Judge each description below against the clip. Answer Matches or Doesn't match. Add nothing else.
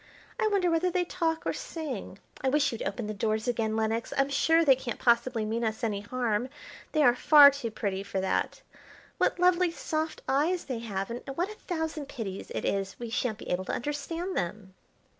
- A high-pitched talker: Matches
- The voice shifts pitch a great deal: Matches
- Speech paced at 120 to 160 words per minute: Doesn't match